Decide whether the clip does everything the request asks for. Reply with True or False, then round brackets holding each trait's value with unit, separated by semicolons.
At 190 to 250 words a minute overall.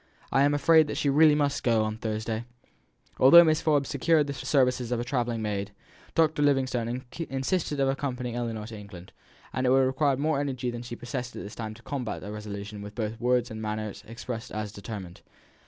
True (205 wpm)